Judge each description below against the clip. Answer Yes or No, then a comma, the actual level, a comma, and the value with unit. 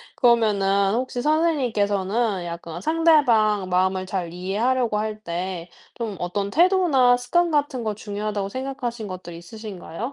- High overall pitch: Yes, high, 215 Hz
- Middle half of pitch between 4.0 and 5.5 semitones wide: Yes, average, 4.9 semitones